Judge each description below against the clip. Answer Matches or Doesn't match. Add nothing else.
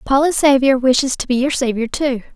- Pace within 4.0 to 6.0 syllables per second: Matches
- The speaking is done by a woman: Matches